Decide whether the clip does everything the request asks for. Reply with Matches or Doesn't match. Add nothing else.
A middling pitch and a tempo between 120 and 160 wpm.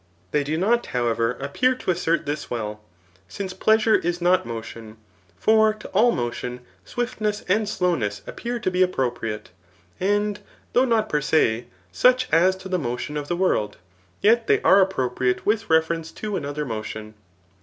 Doesn't match